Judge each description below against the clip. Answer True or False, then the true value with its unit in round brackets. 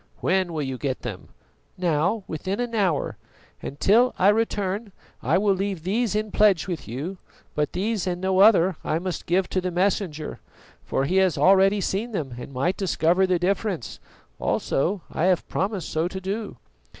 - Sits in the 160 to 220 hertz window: True (185 Hz)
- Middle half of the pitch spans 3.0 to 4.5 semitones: True (3.4 semitones)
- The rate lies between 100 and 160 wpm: False (175 wpm)